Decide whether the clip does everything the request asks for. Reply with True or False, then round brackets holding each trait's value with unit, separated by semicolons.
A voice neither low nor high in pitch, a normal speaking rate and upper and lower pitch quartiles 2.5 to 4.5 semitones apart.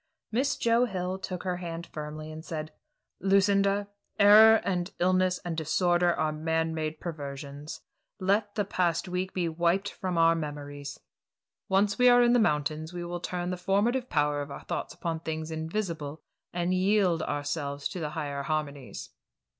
True (175 Hz; 160 wpm; 3.7 semitones)